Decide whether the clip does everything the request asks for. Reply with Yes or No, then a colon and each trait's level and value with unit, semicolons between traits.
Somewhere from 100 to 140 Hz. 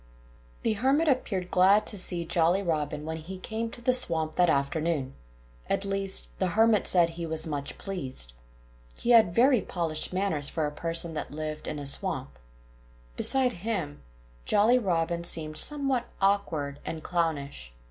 No: medium, 170 Hz